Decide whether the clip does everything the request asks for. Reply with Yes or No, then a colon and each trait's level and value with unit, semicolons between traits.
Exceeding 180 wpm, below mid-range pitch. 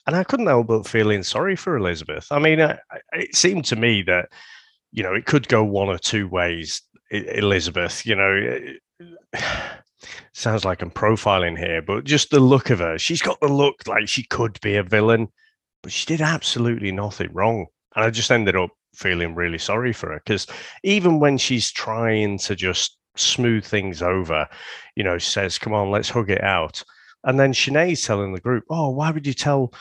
Yes: average, 200 wpm; low, 110 Hz